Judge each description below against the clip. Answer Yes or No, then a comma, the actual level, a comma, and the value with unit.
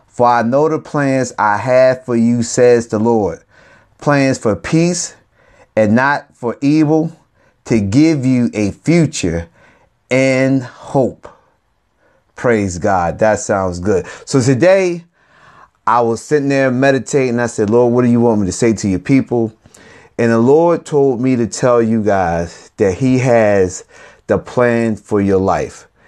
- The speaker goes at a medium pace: Yes, average, 155 wpm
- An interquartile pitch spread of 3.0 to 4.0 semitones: Yes, average, 3.7 semitones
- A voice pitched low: Yes, low, 120 Hz